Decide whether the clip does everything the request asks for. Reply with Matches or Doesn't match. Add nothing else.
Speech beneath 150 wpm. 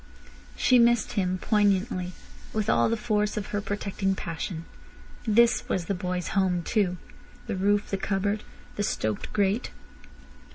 Matches